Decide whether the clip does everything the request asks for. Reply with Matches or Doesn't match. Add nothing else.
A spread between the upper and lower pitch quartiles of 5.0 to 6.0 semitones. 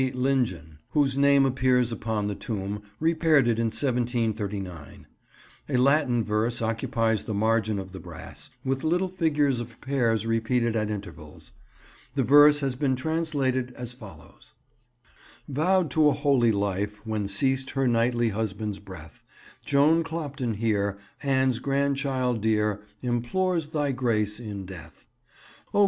Doesn't match